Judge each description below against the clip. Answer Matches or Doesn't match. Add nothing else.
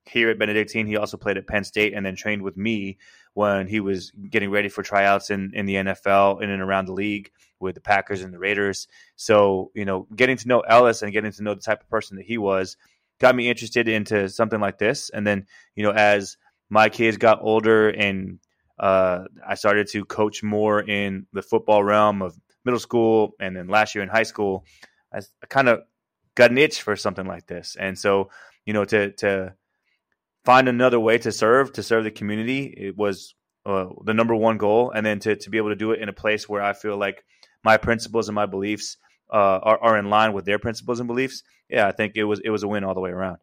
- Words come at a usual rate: Doesn't match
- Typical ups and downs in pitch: Doesn't match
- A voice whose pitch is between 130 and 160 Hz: Doesn't match